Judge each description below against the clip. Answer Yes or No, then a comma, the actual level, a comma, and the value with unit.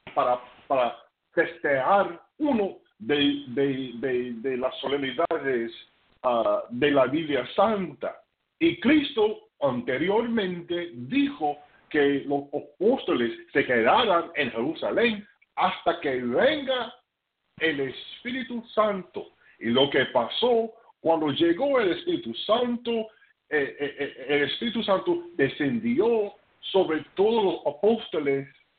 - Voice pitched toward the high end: Yes, high, 195 Hz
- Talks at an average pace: No, slow, 105 wpm